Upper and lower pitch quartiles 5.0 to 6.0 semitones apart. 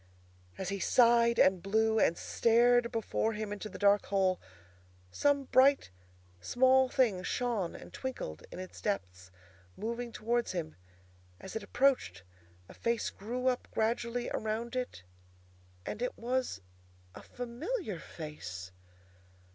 No: average, 4.2 semitones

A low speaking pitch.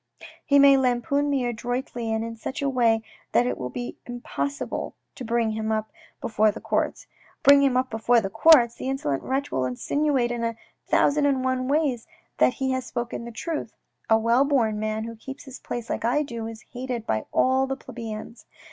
No: high, 245 Hz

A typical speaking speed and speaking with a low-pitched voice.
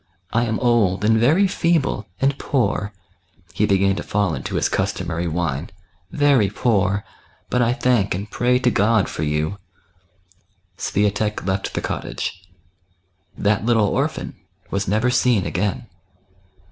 Yes: average, 150 wpm; low, 105 Hz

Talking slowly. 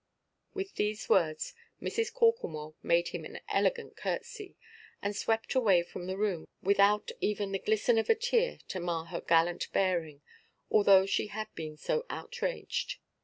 No: average, 155 wpm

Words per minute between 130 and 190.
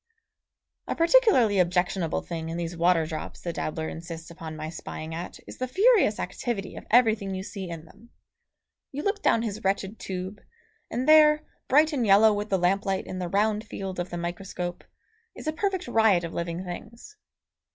Yes: average, 180 wpm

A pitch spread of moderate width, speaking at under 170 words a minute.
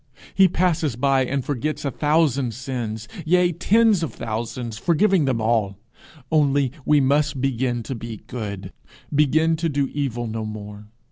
Yes: average, 5.0 semitones; average, 150 wpm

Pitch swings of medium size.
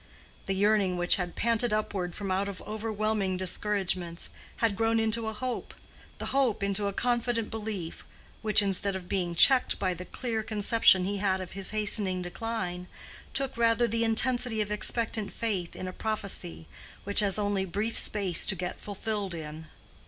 Yes: average, 3.1 semitones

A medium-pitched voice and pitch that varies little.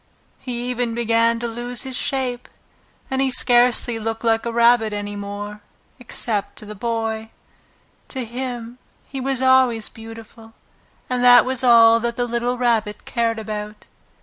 No: high, 235 Hz; narrow, 1.7 semitones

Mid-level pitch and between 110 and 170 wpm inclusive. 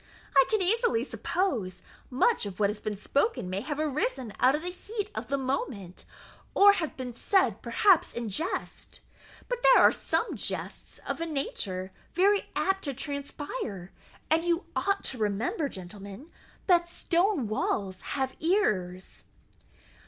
No: very high, 280 Hz; average, 150 wpm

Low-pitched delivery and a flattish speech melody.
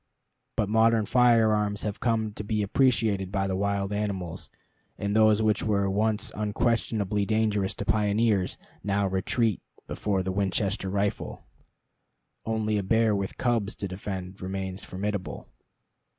Yes: low, 105 Hz; narrow, 2.0 semitones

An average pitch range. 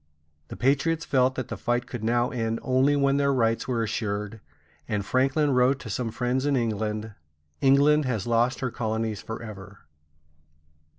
Yes: average, 3.2 semitones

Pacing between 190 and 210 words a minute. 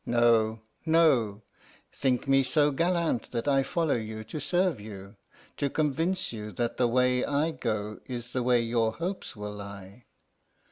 No: average, 155 wpm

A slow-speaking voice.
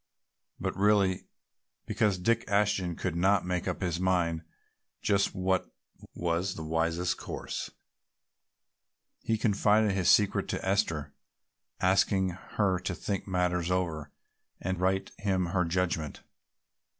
Yes: slow, 120 wpm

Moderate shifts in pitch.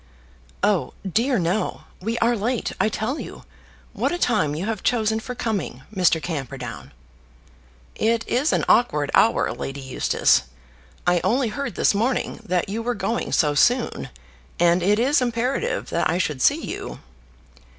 No: wide, 5.7 semitones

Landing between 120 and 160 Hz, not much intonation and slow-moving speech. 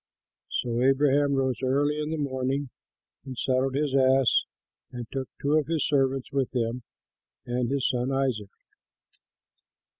No: low, 135 Hz; narrow, 1.6 semitones; average, 145 wpm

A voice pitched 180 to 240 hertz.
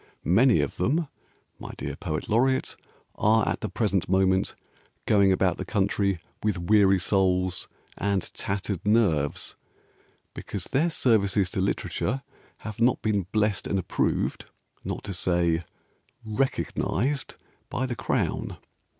No: low, 100 Hz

